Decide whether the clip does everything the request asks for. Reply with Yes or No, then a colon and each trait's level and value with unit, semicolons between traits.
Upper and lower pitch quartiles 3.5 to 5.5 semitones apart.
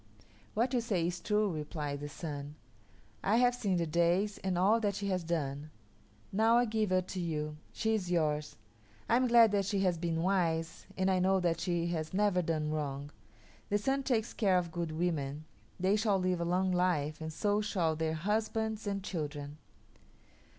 Yes: average, 4.4 semitones